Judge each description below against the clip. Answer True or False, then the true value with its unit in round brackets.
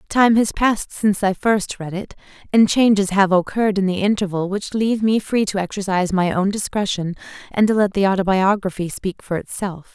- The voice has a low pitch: False (200 Hz)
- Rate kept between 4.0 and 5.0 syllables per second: False (5.6 syllables/s)